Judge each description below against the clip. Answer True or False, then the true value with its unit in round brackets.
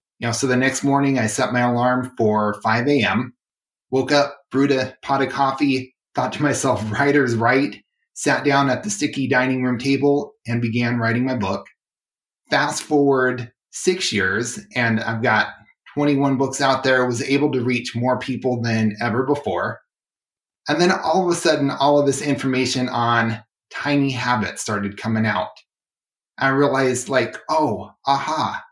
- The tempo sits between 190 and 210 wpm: False (165 wpm)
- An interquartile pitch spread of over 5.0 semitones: False (2.7 semitones)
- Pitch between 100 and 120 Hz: False (130 Hz)